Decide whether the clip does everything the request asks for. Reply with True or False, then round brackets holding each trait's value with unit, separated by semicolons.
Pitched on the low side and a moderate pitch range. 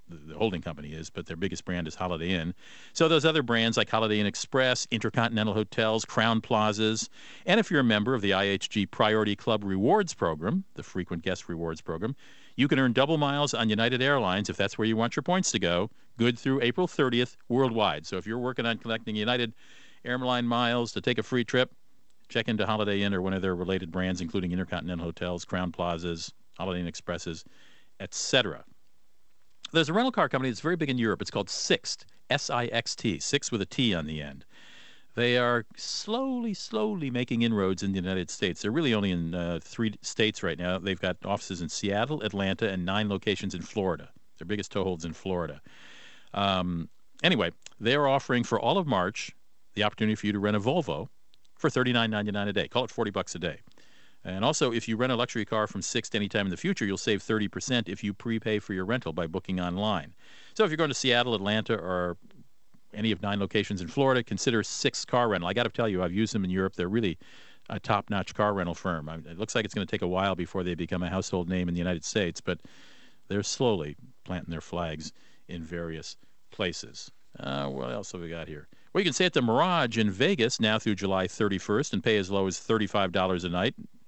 True (105 Hz; 4.6 semitones)